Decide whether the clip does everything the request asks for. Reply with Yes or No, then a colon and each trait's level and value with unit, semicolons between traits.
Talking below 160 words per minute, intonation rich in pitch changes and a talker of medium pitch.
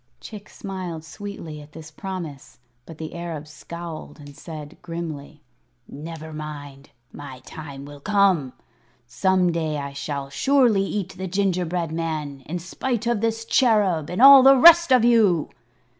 No: average, 145 wpm; average, 4.9 semitones; medium, 170 Hz